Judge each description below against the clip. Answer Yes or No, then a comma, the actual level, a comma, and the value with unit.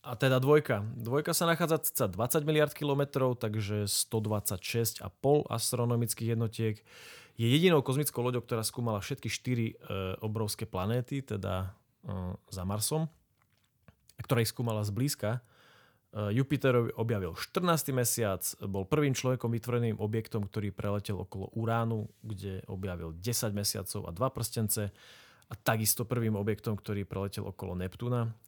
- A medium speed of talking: Yes, average, 135 wpm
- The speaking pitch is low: Yes, low, 115 Hz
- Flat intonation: No, average, 3.4 semitones